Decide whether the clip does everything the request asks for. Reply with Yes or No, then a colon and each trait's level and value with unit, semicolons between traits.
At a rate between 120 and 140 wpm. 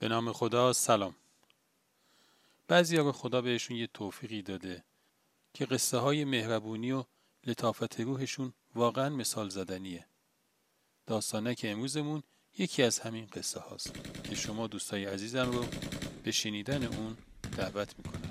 Yes: average, 130 wpm